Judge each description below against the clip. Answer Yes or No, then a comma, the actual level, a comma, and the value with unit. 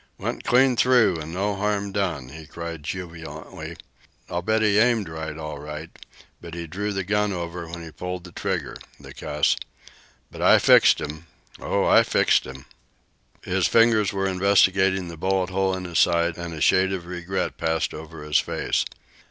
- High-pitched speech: No, very low, 90 Hz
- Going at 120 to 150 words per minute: No, average, 180 wpm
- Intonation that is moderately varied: Yes, average, 3.3 semitones